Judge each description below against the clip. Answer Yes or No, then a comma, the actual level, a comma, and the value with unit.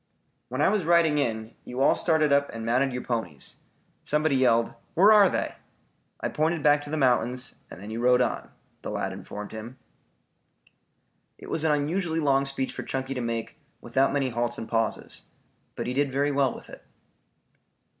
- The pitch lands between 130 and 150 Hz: Yes, low, 135 Hz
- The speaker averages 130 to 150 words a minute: No, average, 185 wpm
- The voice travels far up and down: No, average, 3.9 semitones